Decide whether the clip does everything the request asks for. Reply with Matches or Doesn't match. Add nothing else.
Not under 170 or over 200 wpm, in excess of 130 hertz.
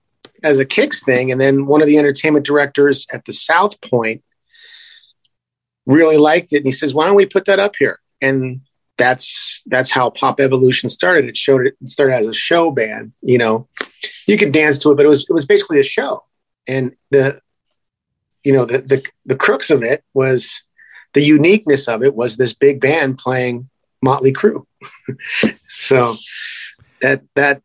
Matches